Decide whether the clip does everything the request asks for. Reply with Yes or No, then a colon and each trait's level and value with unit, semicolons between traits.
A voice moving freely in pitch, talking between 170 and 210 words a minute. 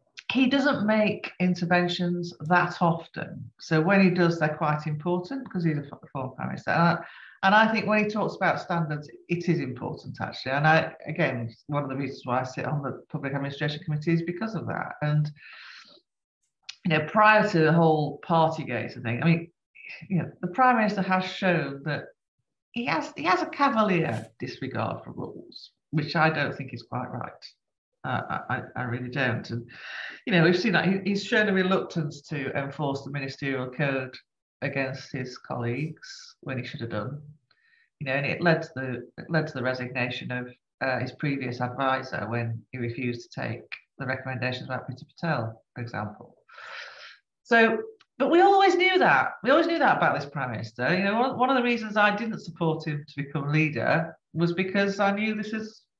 Yes: wide, 6.4 semitones; average, 195 wpm